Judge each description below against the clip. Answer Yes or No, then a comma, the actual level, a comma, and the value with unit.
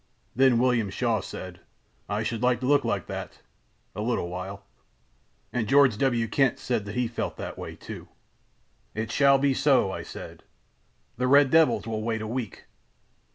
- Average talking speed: Yes, average, 165 wpm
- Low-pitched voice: Yes, low, 120 Hz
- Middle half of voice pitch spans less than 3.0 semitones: No, average, 3.7 semitones